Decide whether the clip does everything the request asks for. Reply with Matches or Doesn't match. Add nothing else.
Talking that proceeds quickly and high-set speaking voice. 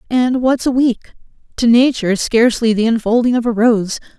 Doesn't match